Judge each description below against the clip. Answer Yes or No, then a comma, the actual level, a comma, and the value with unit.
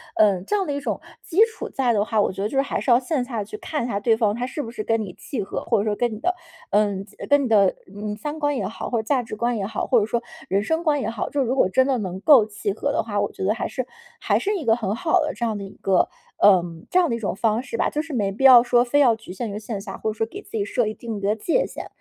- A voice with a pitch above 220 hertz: Yes, high, 230 Hz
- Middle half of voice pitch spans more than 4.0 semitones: Yes, average, 4.4 semitones